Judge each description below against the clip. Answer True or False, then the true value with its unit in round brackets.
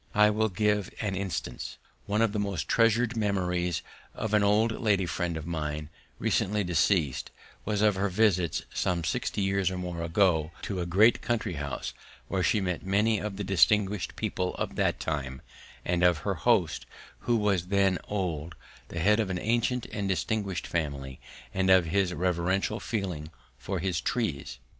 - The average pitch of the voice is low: True (95 Hz)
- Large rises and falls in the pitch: False (3.4 semitones)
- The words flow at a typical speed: True (170 wpm)